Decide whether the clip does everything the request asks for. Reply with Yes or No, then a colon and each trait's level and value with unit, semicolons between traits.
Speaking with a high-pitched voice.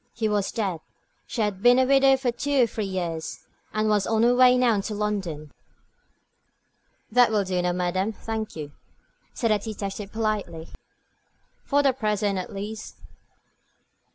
Yes: high, 215 Hz